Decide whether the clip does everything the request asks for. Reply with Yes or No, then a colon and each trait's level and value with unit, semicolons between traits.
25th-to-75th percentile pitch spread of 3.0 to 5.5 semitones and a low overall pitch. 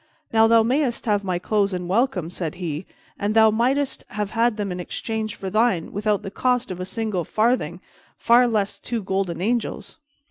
No: average, 3.8 semitones; high, 210 Hz